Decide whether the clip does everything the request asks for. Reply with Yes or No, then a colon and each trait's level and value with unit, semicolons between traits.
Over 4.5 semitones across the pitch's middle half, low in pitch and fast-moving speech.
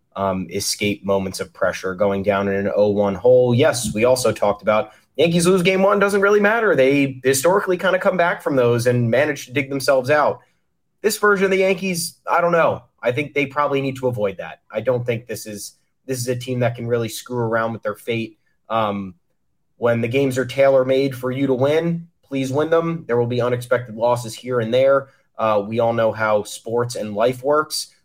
Yes: average, 5.2 semitones; low, 125 Hz; fast, 220 wpm